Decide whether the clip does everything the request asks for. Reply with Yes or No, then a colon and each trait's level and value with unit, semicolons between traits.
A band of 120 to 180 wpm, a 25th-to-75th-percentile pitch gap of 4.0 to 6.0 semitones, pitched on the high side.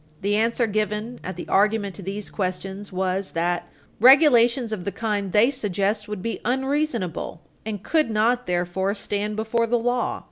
No: average, 165 wpm; average, 3.3 semitones; high, 210 Hz